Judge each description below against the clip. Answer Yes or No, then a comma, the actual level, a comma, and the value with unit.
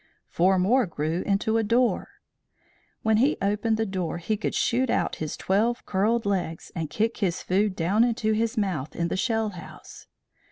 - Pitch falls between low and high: No, high, 205 Hz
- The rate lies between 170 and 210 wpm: Yes, average, 175 wpm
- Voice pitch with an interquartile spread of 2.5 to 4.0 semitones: Yes, average, 3.7 semitones